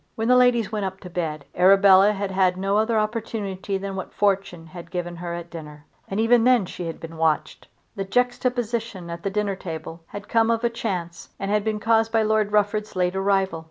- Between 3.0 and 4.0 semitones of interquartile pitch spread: Yes, average, 3.7 semitones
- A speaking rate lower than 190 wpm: No, fast, 205 wpm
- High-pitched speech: Yes, high, 195 Hz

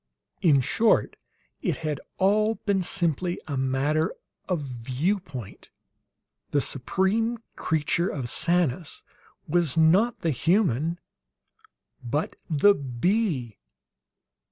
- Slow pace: Yes, slow, 100 wpm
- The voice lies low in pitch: No, medium, 160 Hz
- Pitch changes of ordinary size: No, wide, 5.7 semitones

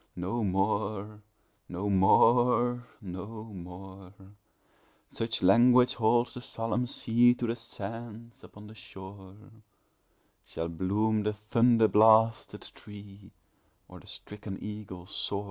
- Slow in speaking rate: Yes, slow, 110 wpm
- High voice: No, low, 105 Hz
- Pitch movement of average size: Yes, average, 3.1 semitones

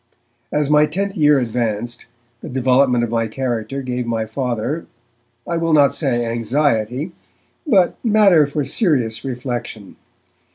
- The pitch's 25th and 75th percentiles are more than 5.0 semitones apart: No, average, 4.3 semitones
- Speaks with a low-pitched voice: Yes, low, 130 Hz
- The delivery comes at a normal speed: No, slow, 130 wpm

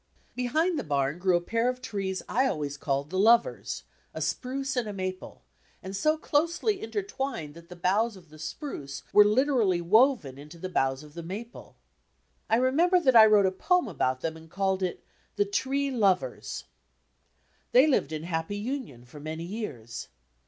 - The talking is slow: No, average, 175 wpm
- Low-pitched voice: No, high, 200 Hz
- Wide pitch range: Yes, wide, 8.2 semitones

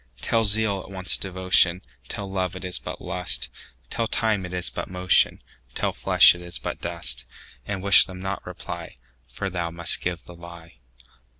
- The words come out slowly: No, average, 155 wpm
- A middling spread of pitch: No, narrow, 2.1 semitones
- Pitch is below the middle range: Yes, very low, 90 Hz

